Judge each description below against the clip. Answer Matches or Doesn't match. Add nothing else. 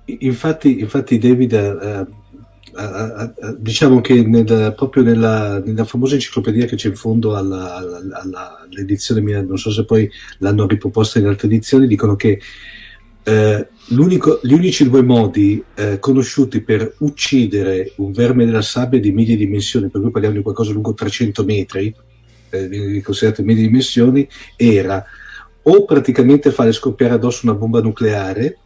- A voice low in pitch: Matches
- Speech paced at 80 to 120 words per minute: Doesn't match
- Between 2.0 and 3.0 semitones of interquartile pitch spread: Doesn't match